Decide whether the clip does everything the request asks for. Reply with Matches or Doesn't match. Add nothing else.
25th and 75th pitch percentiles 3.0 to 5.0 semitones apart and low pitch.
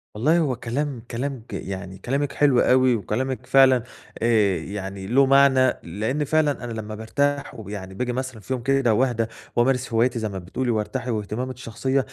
Matches